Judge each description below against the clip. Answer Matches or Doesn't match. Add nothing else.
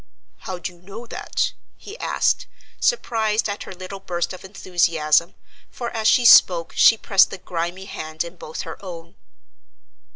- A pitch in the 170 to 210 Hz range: Matches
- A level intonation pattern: Doesn't match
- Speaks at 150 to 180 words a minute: Matches